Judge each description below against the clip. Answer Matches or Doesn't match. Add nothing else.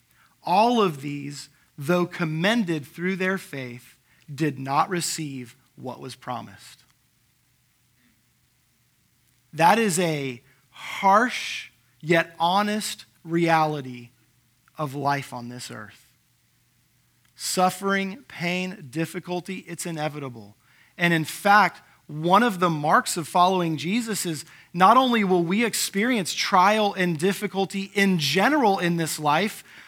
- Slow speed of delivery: Matches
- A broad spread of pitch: Matches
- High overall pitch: Doesn't match